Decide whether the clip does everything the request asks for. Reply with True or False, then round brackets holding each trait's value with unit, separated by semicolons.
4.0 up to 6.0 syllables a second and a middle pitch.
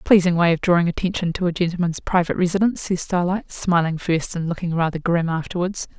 False (6.2 syllables/s; 175 Hz)